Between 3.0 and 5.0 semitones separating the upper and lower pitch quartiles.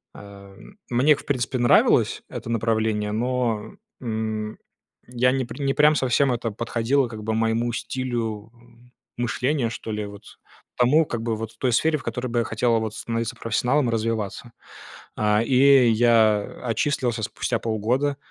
No: narrow, 2.4 semitones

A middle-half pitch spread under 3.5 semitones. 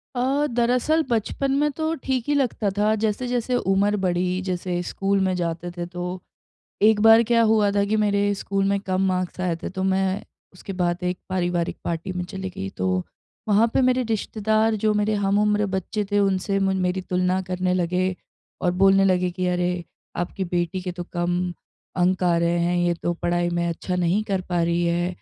Yes: average, 2.9 semitones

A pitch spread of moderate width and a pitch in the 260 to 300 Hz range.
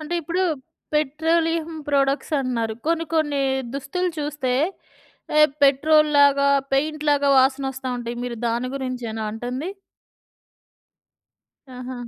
Yes: average, 3.2 semitones; very high, 280 Hz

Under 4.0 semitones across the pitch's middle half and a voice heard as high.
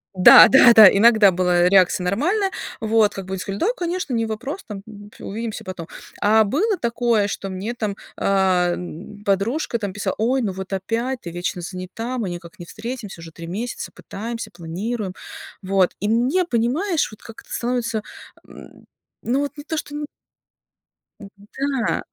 No: average, 4.3 semitones; high, 215 Hz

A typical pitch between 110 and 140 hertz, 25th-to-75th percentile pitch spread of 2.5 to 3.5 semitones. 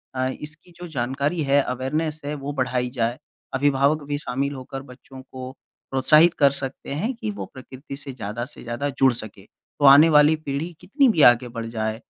Yes: low, 135 Hz; average, 2.8 semitones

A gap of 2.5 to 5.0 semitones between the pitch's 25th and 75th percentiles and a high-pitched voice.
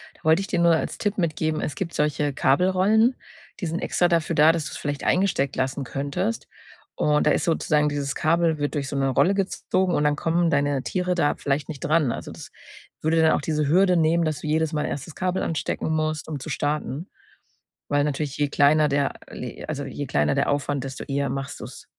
No: average, 2.9 semitones; medium, 155 Hz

